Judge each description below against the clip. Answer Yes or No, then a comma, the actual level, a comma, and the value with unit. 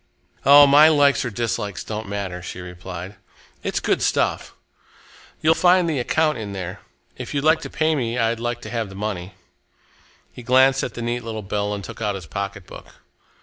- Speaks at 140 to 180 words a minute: No, average, 190 wpm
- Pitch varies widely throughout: Yes, wide, 5.8 semitones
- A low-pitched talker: Yes, low, 115 Hz